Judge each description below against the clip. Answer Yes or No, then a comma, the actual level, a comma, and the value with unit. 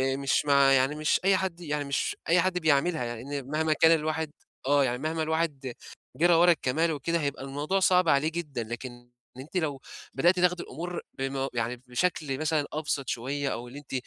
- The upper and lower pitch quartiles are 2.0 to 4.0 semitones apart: Yes, average, 3.5 semitones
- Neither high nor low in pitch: Yes, medium, 150 Hz